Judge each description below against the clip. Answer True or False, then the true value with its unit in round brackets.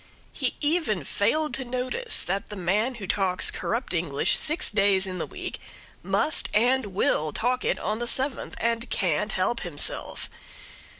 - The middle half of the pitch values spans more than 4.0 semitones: True (5.3 semitones)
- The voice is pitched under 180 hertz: False (215 Hz)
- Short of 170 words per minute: True (160 wpm)